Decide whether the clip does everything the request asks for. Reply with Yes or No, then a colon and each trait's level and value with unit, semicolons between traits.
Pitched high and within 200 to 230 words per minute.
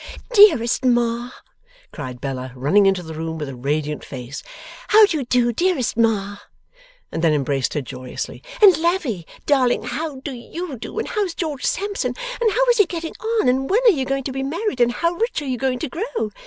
Yes: very high, 255 Hz; fast, 205 wpm